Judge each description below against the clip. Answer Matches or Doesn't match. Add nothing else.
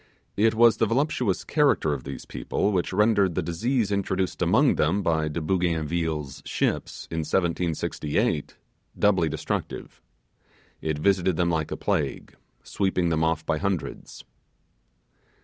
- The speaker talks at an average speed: Doesn't match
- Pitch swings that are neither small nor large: Matches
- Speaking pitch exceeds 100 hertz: Doesn't match